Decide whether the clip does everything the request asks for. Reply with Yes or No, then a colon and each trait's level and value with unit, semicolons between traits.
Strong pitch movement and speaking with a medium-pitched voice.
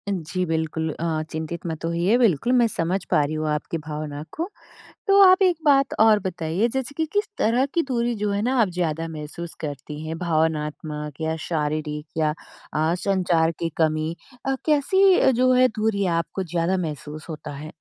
Yes: wide, 6.2 semitones; medium, 165 Hz